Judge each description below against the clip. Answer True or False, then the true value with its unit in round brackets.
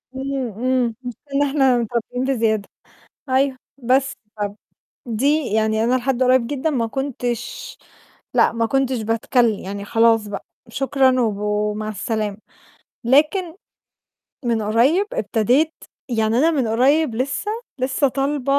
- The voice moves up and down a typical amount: True (3.5 semitones)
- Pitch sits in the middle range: False (250 Hz)